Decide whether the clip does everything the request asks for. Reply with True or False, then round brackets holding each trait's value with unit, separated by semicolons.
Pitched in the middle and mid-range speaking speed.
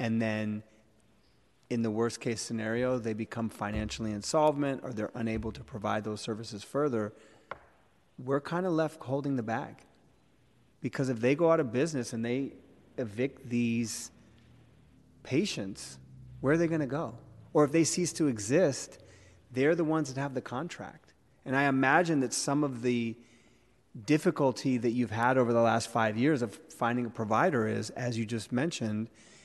False (120 Hz; 165 wpm)